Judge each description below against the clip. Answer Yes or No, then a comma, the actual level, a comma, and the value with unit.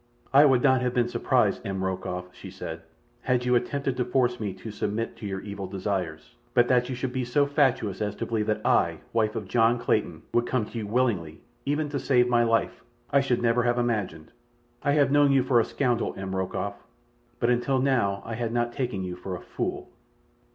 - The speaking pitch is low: Yes, low, 120 Hz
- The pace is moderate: No, fast, 215 wpm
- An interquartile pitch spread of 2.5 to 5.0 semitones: Yes, average, 3.9 semitones